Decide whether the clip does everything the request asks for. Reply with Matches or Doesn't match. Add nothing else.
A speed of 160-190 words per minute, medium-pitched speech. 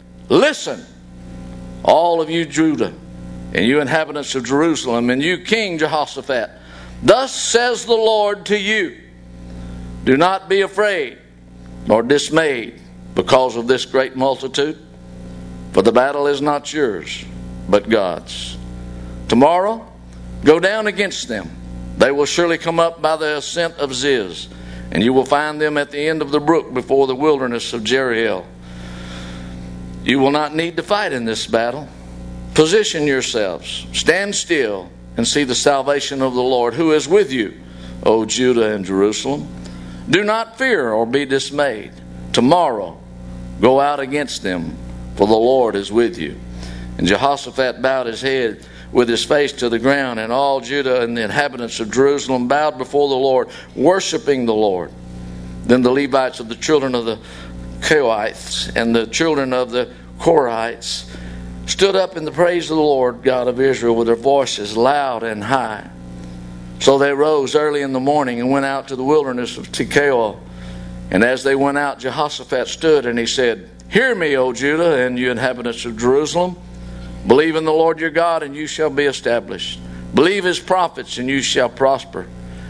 Doesn't match